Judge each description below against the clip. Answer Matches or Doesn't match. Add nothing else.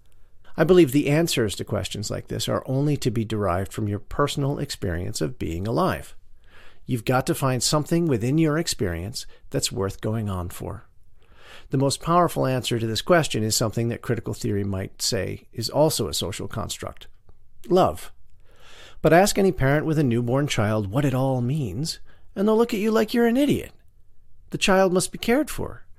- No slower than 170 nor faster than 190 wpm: Matches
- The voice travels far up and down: Matches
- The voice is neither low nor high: Doesn't match